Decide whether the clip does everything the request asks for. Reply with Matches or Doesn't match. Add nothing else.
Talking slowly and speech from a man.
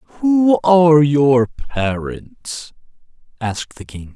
Matches